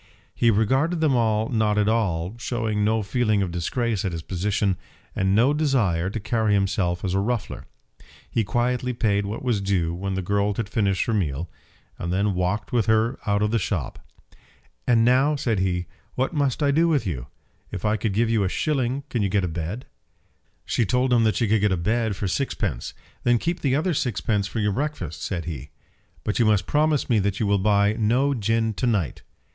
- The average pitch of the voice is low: Yes, low, 105 Hz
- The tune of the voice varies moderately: Yes, average, 3.8 semitones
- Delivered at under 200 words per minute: No, fast, 205 wpm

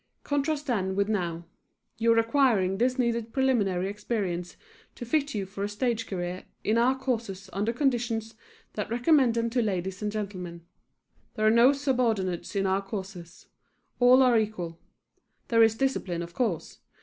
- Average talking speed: Yes, average, 160 wpm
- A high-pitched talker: Yes, high, 220 Hz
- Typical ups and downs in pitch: Yes, average, 4.3 semitones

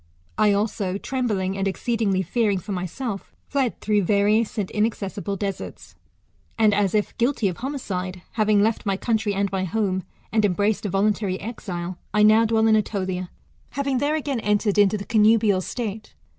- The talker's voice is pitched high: Yes, high, 210 Hz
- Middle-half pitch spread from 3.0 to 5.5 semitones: No, narrow, 2.4 semitones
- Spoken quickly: No, average, 170 wpm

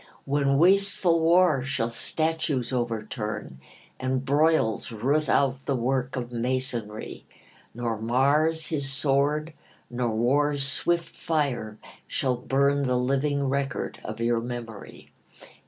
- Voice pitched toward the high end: No, low, 135 Hz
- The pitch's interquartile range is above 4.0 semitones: No, average, 3.5 semitones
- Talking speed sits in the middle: No, slow, 115 wpm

